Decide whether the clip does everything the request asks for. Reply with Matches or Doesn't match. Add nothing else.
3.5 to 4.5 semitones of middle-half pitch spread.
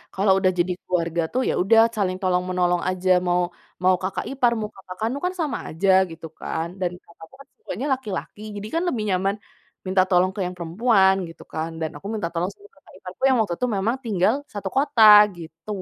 Matches